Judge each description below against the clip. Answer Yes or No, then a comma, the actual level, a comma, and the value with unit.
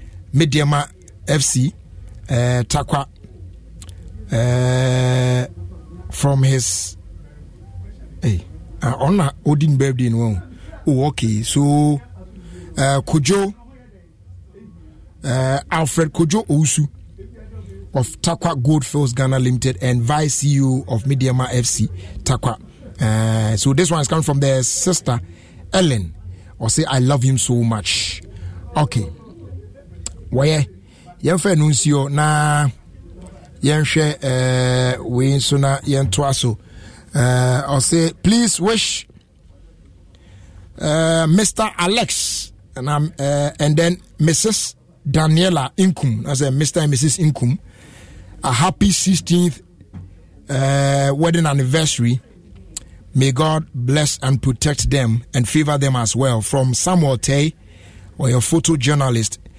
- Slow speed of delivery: Yes, slow, 100 wpm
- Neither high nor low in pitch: No, low, 130 Hz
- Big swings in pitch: Yes, wide, 7.4 semitones